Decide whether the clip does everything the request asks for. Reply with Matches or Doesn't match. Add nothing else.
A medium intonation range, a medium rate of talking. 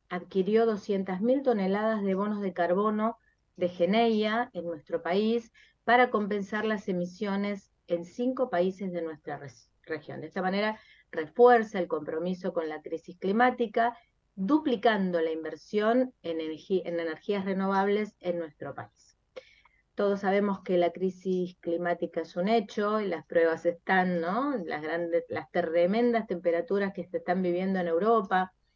Matches